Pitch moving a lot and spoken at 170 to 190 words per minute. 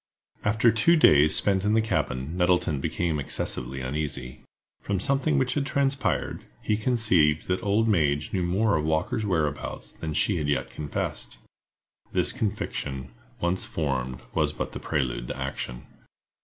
No: wide, 6.8 semitones; average, 155 wpm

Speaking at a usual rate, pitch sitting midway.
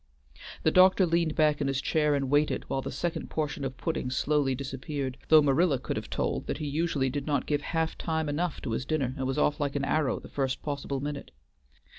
No: fast, 220 wpm; medium, 145 Hz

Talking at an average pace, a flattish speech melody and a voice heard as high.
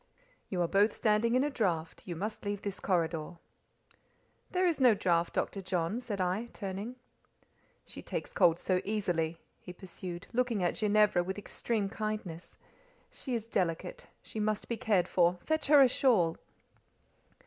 No: average, 160 wpm; average, 4.3 semitones; high, 200 Hz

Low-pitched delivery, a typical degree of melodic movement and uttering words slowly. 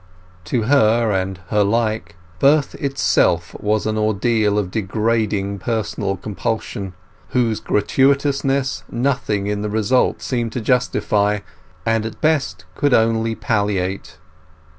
Yes: low, 110 Hz; average, 3.1 semitones; slow, 120 wpm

